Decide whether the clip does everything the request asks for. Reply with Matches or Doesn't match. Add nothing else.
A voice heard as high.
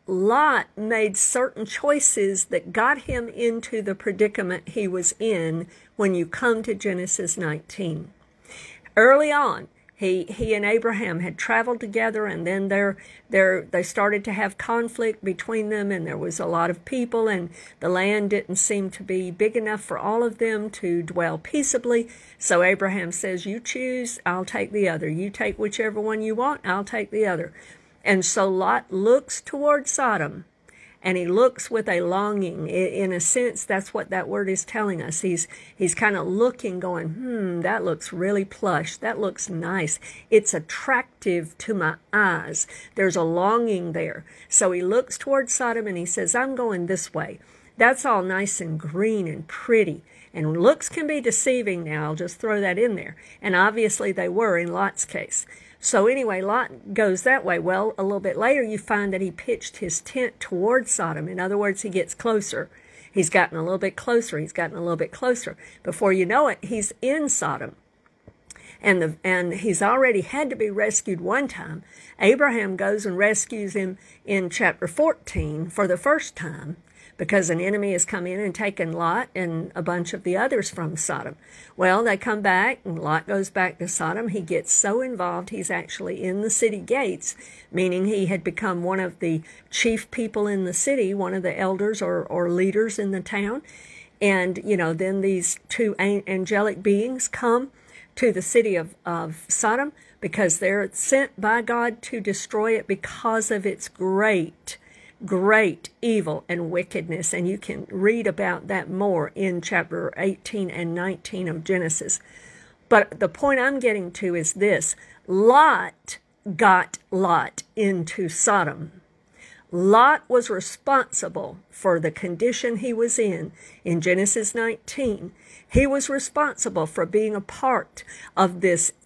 Matches